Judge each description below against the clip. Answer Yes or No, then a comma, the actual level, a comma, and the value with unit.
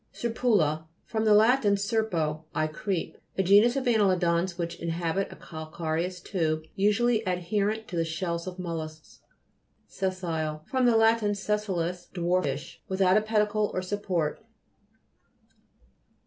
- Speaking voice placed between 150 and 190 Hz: Yes, medium, 185 Hz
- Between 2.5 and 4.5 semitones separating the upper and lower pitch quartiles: Yes, average, 4.0 semitones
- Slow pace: Yes, slow, 120 wpm